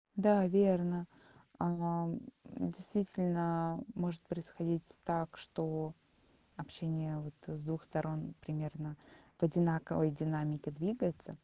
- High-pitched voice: No, medium, 165 Hz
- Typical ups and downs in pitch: No, narrow, 1.9 semitones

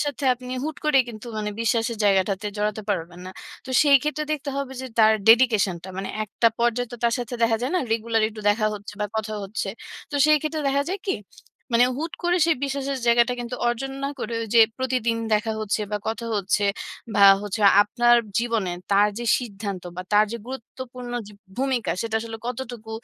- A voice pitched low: No, high, 235 Hz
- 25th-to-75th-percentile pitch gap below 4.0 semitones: Yes, average, 3.5 semitones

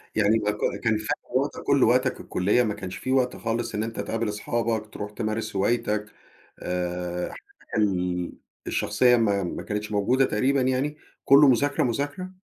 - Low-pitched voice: Yes, low, 110 Hz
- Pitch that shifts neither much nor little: Yes, average, 3.2 semitones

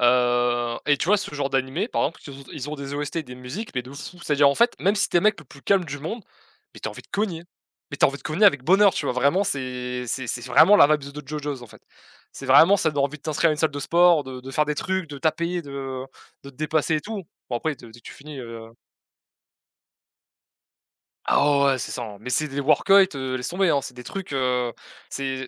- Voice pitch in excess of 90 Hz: Yes, medium, 140 Hz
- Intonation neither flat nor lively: Yes, average, 4.2 semitones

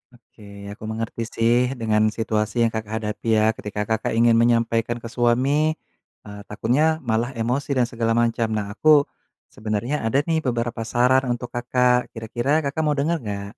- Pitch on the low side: Yes, low, 120 Hz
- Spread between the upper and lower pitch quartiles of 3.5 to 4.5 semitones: No, average, 2.7 semitones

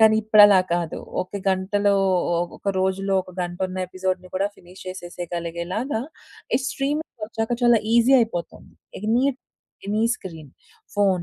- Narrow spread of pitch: No, average, 3.1 semitones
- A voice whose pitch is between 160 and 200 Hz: Yes, high, 195 Hz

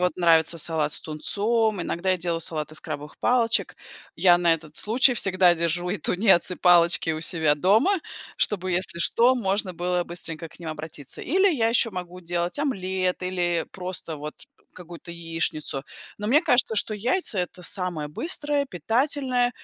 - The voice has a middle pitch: Yes, medium, 180 Hz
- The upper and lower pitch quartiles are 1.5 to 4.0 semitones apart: No, average, 4.8 semitones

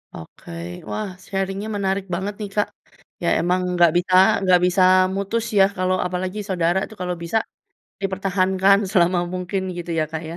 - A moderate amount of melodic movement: No, narrow, 1.6 semitones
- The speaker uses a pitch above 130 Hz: Yes, medium, 185 Hz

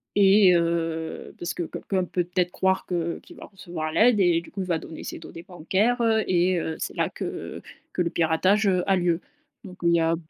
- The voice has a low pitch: No, medium, 180 Hz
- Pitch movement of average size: No, narrow, 2.3 semitones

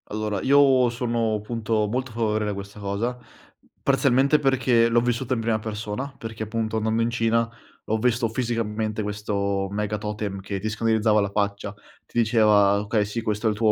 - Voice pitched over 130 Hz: No, low, 110 Hz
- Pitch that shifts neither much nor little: No, narrow, 1.9 semitones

